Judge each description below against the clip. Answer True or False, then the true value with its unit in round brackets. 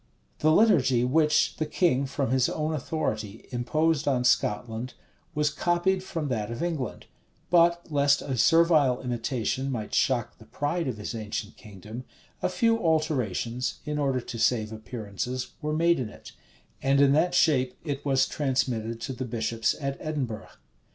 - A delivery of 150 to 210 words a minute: True (160 wpm)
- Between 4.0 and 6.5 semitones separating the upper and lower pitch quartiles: True (4.7 semitones)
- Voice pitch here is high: False (135 Hz)